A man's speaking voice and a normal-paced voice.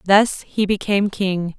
No: female; average, 150 wpm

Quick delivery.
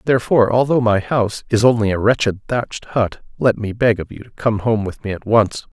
Yes: fast, 230 wpm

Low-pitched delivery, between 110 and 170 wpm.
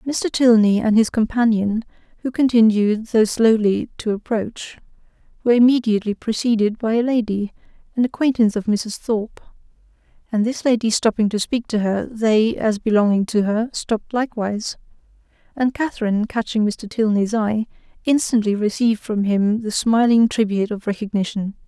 No: high, 220 Hz; average, 145 wpm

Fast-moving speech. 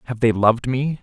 Yes: fast, 235 wpm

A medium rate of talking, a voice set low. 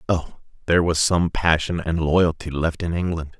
Yes: average, 175 wpm; very low, 80 Hz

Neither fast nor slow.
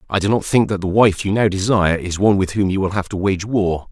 No: fast, 305 wpm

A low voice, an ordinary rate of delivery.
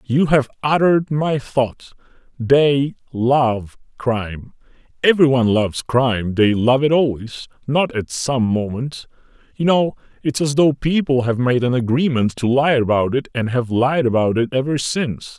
Yes: low, 130 Hz; average, 160 wpm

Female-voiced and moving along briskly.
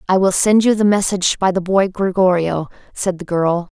Yes: female; fast, 210 wpm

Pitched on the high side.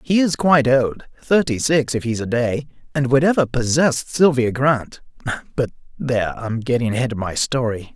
No: low, 130 Hz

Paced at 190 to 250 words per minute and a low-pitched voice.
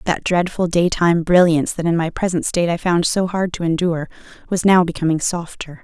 No: average, 195 wpm; medium, 170 Hz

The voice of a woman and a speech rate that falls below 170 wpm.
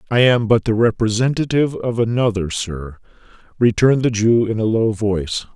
No: male; average, 160 wpm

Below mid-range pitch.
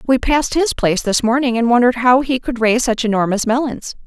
No: high, 245 Hz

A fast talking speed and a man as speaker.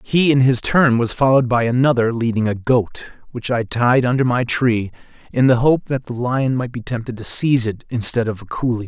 Yes: fast, 225 wpm; male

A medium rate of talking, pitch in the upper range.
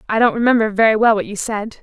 No: fast, 265 wpm; high, 220 Hz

